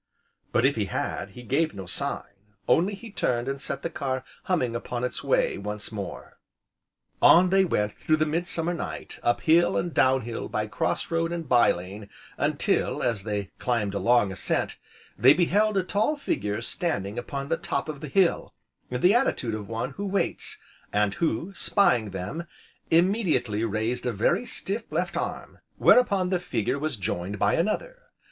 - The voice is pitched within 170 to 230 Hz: No, low, 130 Hz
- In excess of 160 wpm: Yes, average, 175 wpm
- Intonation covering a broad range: Yes, wide, 8.3 semitones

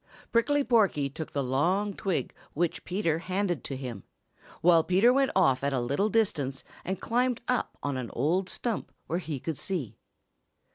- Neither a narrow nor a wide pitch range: No, wide, 6.8 semitones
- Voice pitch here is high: No, medium, 175 Hz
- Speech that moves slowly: No, average, 170 wpm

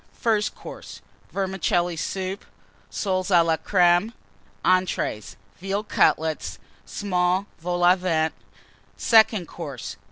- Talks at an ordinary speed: No, slow, 100 wpm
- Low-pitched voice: No, medium, 185 Hz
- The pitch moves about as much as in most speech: No, narrow, 2.3 semitones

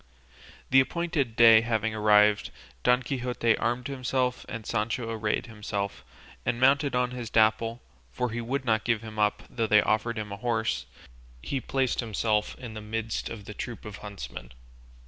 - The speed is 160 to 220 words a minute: Yes, average, 165 wpm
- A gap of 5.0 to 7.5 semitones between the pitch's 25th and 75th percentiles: No, narrow, 2.6 semitones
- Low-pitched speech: Yes, low, 115 Hz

